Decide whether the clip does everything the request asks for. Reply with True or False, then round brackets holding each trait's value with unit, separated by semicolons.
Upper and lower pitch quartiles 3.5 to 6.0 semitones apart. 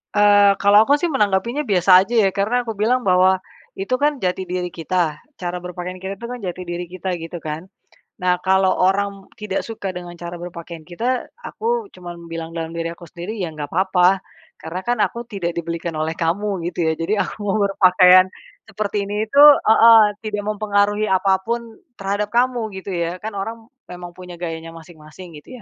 False (3.0 semitones)